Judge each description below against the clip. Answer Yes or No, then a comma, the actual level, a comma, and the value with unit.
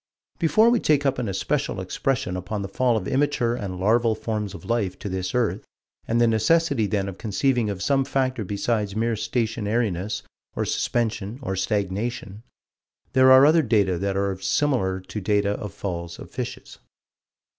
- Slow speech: No, average, 165 wpm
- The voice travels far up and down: No, average, 4.1 semitones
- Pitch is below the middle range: Yes, low, 110 Hz